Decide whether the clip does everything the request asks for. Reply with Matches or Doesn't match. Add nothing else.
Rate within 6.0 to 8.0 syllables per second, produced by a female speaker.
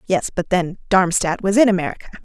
Matches